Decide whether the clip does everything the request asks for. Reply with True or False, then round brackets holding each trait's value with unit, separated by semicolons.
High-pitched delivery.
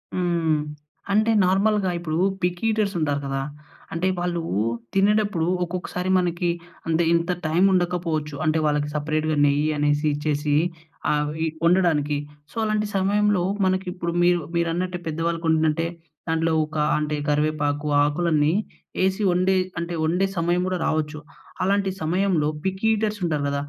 False (170 Hz)